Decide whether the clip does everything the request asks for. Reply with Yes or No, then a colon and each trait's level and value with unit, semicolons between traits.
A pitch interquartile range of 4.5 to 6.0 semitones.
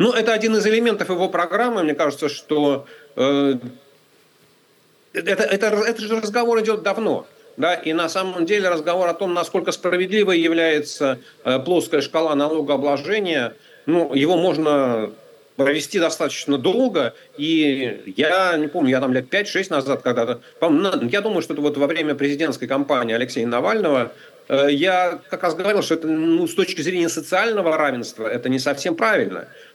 Yes: average, 5.2 semitones